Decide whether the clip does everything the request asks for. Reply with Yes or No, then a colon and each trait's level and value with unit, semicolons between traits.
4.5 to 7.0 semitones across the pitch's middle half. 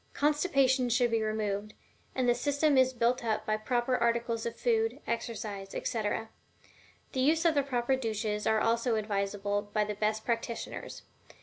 No: average, 2.8 semitones